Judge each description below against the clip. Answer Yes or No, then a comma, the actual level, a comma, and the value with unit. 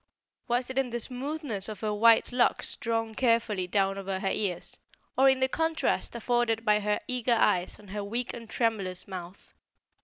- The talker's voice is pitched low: No, high, 225 Hz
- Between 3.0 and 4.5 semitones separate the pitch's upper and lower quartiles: Yes, average, 3.5 semitones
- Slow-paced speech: No, average, 180 wpm